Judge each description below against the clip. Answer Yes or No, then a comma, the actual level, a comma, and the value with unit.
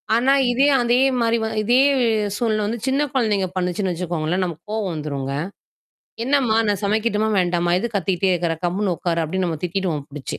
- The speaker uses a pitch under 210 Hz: Yes, high, 190 Hz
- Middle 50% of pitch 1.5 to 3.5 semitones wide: No, average, 4.3 semitones